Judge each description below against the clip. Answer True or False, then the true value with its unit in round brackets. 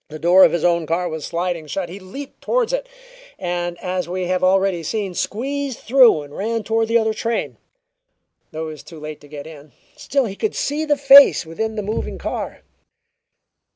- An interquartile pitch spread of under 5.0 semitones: False (5.5 semitones)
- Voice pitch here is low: False (185 Hz)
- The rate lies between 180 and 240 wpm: True (195 wpm)